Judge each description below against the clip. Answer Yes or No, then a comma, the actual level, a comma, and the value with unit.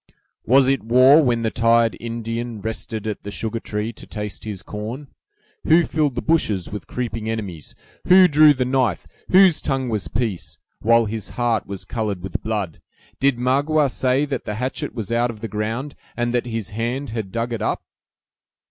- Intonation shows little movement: No, average, 3.3 semitones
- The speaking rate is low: No, average, 180 wpm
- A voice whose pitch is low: Yes, low, 115 Hz